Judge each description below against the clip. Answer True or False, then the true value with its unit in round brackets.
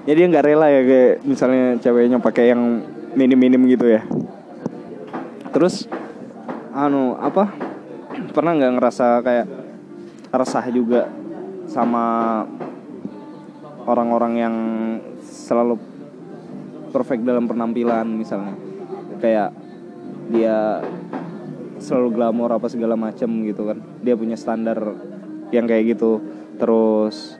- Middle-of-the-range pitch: False (120 Hz)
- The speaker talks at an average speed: True (100 wpm)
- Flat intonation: True (1.7 semitones)